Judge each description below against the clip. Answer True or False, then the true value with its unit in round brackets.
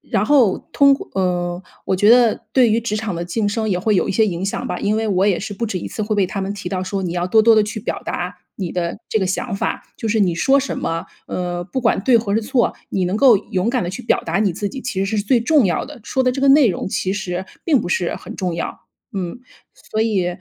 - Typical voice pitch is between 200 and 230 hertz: True (205 Hz)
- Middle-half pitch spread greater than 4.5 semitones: False (3.8 semitones)